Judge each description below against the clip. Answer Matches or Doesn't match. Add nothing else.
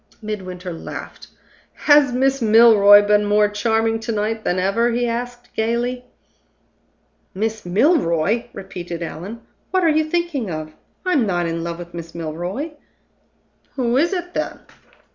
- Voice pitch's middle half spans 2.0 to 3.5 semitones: Doesn't match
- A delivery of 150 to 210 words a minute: Doesn't match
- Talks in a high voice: Matches